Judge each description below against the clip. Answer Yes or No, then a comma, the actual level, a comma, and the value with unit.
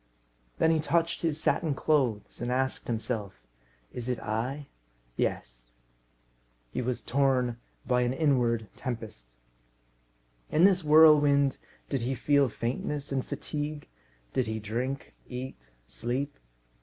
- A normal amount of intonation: Yes, average, 3.9 semitones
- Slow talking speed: Yes, slow, 120 wpm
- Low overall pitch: Yes, low, 130 Hz